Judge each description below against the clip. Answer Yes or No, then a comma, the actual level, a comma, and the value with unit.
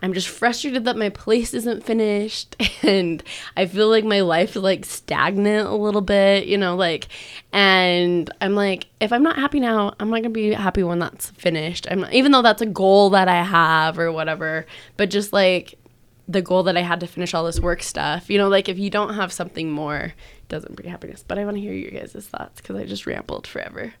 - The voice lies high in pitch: Yes, high, 195 Hz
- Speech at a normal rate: No, fast, 230 wpm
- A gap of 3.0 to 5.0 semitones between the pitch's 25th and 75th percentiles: Yes, average, 3.4 semitones